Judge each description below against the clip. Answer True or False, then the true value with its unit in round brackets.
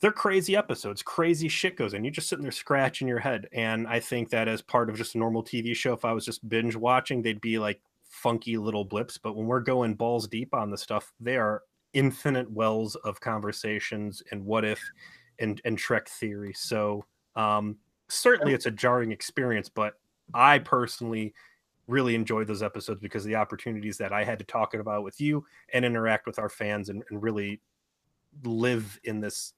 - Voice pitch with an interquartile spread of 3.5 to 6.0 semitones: False (2.4 semitones)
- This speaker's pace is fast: False (195 wpm)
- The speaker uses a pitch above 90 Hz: True (115 Hz)